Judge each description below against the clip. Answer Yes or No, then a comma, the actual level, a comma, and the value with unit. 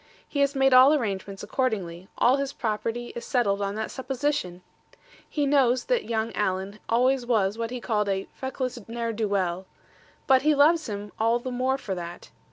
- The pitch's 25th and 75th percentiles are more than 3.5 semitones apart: Yes, average, 4.6 semitones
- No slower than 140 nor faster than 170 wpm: No, average, 180 wpm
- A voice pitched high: Yes, high, 235 Hz